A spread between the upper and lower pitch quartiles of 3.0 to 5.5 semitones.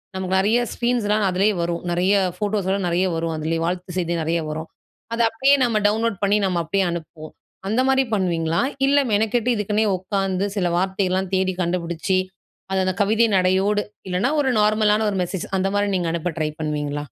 Yes: average, 3.4 semitones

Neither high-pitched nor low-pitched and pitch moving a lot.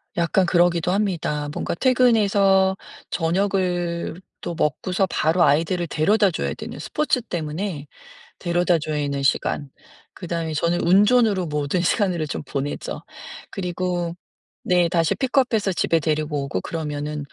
No: medium, 175 Hz; average, 3.7 semitones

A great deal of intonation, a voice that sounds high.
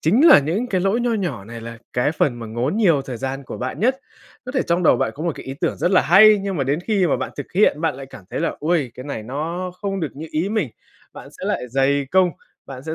No: wide, 6.4 semitones; medium, 160 Hz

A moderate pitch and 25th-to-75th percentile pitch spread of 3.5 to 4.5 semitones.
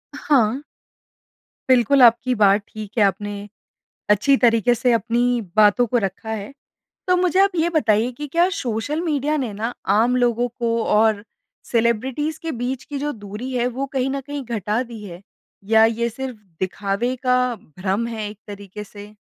No: high, 235 Hz; average, 4.0 semitones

